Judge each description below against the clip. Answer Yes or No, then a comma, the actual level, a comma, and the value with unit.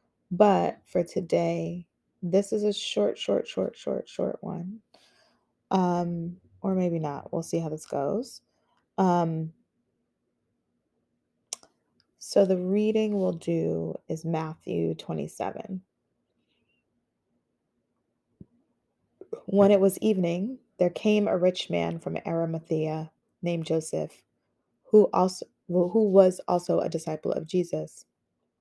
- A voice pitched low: No, medium, 175 Hz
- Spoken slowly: Yes, slow, 115 wpm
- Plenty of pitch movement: No, average, 3.7 semitones